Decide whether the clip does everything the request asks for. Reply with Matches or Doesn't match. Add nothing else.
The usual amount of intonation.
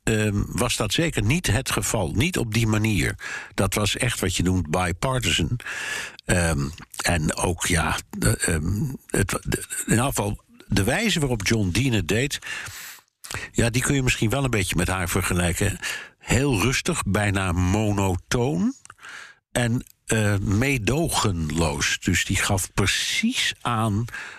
Matches